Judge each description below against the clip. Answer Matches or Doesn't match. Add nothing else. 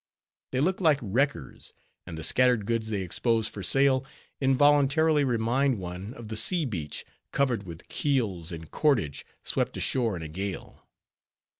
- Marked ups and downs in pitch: Matches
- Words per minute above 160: Doesn't match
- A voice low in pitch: Matches